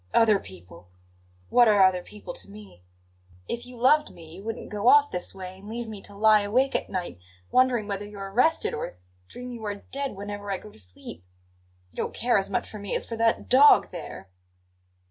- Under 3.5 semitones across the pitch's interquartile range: No, average, 3.8 semitones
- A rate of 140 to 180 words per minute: No, fast, 205 wpm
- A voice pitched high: Yes, high, 210 Hz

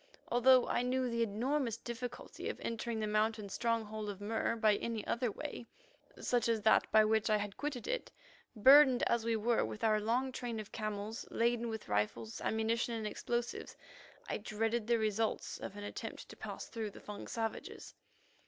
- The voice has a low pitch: No, high, 225 Hz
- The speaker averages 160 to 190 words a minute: Yes, average, 180 wpm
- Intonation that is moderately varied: No, narrow, 1.9 semitones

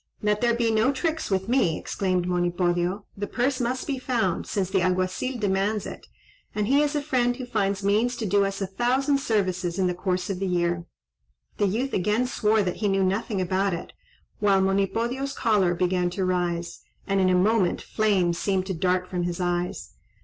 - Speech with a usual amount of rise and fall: Yes, average, 4.1 semitones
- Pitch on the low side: No, high, 195 Hz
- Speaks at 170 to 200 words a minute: Yes, average, 195 wpm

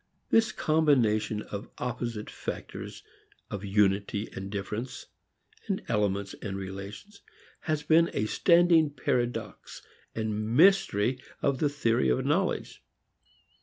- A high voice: No, low, 115 Hz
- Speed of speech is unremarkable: No, slow, 105 wpm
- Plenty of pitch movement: Yes, wide, 6.5 semitones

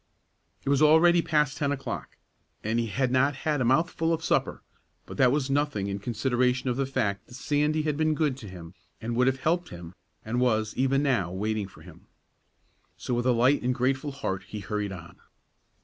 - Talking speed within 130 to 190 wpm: No, average, 200 wpm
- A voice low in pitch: Yes, low, 130 Hz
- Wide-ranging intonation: No, average, 4.9 semitones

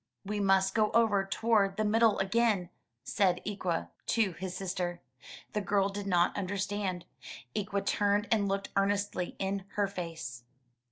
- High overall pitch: Yes, high, 195 Hz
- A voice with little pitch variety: Yes, narrow, 1.6 semitones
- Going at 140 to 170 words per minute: Yes, average, 145 wpm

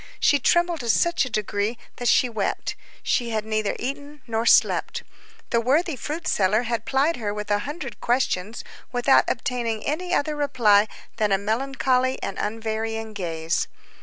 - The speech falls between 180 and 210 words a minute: No, average, 160 wpm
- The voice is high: Yes, high, 235 Hz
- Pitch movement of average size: Yes, average, 4.1 semitones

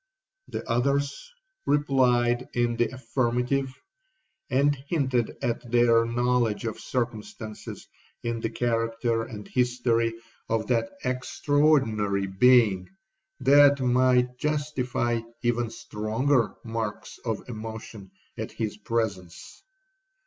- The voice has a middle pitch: No, low, 120 Hz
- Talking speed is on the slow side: Yes, slow, 100 wpm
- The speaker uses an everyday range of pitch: No, narrow, 2.3 semitones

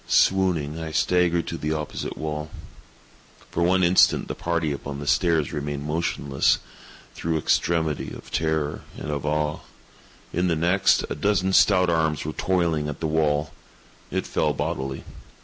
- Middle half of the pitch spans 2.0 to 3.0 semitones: Yes, narrow, 2.5 semitones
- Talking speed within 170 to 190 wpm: No, average, 150 wpm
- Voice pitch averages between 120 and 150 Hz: No, very low, 80 Hz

